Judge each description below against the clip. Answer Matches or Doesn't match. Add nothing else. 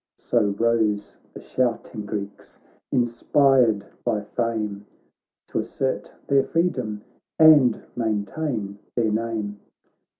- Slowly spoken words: Matches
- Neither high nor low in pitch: Doesn't match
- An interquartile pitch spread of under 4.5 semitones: Matches